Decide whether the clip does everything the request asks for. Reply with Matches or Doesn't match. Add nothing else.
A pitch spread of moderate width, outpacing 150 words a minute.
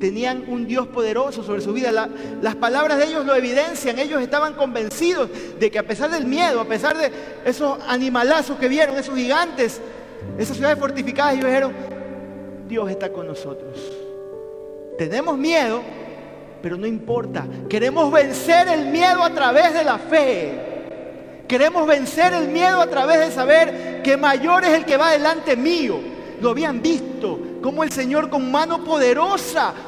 Matches